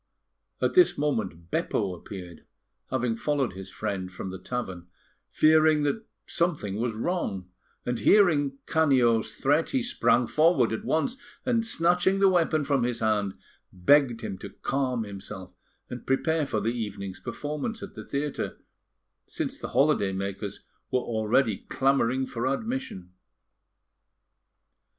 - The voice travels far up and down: Yes, wide, 7.0 semitones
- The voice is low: Yes, low, 125 Hz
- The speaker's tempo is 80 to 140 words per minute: Yes, slow, 135 wpm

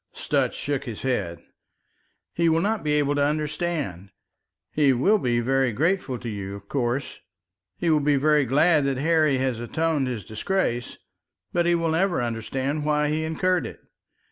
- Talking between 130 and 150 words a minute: No, average, 170 wpm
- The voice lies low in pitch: No, medium, 145 Hz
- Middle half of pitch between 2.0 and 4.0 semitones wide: No, average, 4.6 semitones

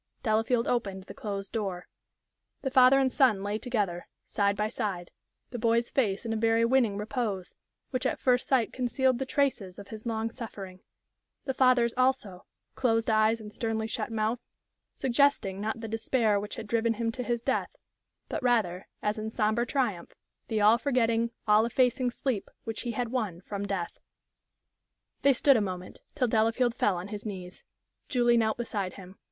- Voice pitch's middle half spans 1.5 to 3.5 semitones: Yes, average, 3.1 semitones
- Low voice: No, high, 225 Hz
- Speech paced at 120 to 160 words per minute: No, average, 175 wpm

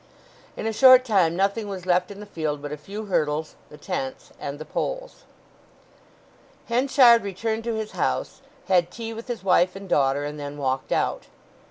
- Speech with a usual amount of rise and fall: No, wide, 6.9 semitones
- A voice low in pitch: No, high, 195 Hz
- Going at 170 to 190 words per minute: Yes, average, 180 wpm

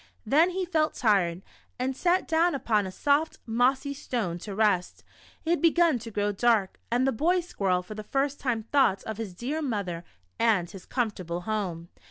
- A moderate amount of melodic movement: No, wide, 6.4 semitones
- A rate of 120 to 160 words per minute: No, average, 185 wpm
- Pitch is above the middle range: Yes, high, 230 Hz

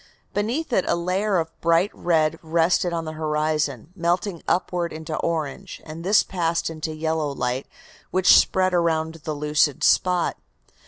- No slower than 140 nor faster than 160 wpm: Yes, average, 150 wpm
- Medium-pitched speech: Yes, medium, 165 Hz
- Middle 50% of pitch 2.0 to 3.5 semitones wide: Yes, narrow, 2.5 semitones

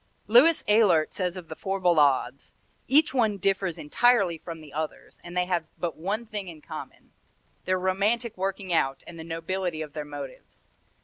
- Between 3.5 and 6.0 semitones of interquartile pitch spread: Yes, average, 4.0 semitones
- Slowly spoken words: No, average, 175 wpm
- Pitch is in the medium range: Yes, medium, 180 Hz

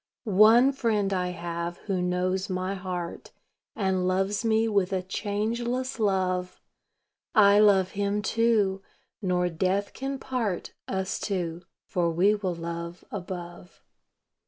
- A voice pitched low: No, high, 190 Hz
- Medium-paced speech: No, slow, 125 wpm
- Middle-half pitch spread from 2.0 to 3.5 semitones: Yes, average, 2.8 semitones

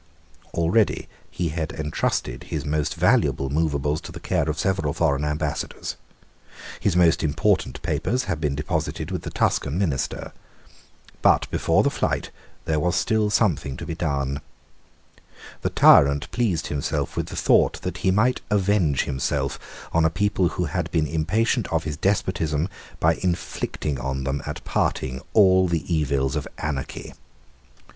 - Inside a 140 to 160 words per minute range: Yes, average, 150 wpm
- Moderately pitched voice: No, very low, 80 Hz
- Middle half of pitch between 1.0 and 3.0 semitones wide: No, average, 4.2 semitones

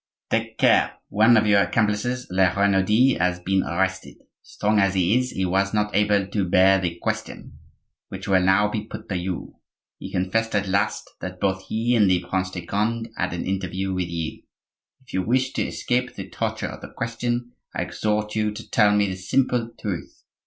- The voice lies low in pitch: Yes, low, 100 Hz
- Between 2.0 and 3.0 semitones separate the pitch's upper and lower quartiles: Yes, average, 2.7 semitones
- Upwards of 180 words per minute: Yes, average, 195 wpm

